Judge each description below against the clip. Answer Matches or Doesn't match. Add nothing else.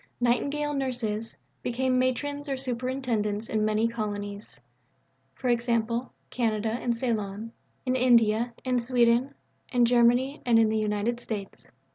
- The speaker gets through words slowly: Matches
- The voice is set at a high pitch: Matches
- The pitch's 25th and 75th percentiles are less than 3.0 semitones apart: Matches